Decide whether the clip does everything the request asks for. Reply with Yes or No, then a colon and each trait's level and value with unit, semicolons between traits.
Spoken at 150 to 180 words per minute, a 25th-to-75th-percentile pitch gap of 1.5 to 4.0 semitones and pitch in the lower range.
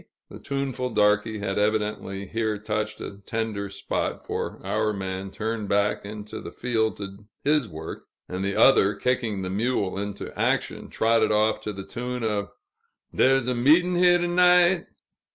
Yes: average, 160 wpm; average, 3.7 semitones; low, 110 Hz